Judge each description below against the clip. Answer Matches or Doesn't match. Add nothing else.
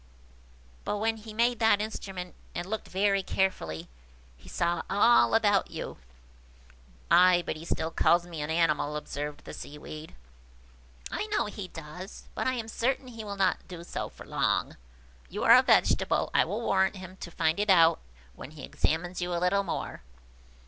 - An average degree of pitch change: Matches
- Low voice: Doesn't match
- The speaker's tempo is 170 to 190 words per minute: Matches